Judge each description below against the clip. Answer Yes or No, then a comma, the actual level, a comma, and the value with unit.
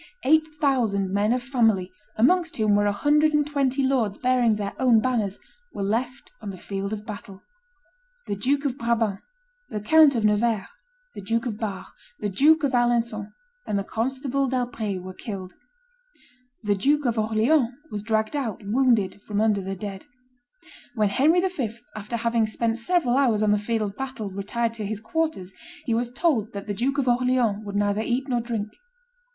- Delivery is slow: No, average, 180 wpm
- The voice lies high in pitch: Yes, high, 225 Hz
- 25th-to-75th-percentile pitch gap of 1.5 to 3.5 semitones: No, average, 4.0 semitones